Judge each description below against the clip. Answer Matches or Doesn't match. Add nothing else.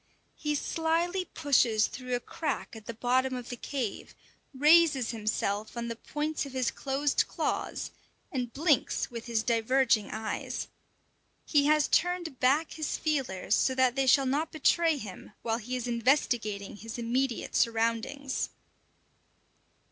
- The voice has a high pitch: Matches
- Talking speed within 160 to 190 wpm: Doesn't match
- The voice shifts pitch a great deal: Doesn't match